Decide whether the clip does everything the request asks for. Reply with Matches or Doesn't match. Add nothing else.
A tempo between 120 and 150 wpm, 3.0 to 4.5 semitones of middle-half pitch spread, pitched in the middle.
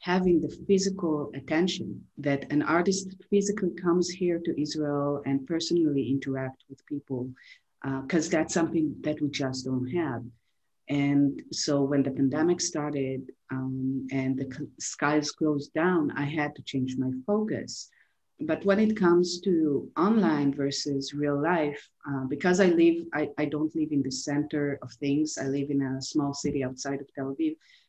Doesn't match